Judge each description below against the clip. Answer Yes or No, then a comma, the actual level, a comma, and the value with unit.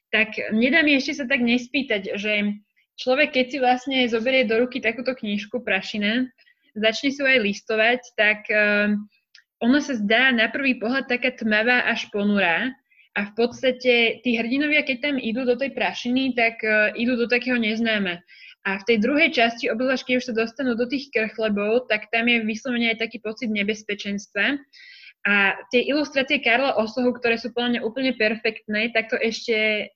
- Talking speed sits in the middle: No, fast, 170 wpm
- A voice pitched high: Yes, high, 235 Hz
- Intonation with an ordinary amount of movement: Yes, average, 3.0 semitones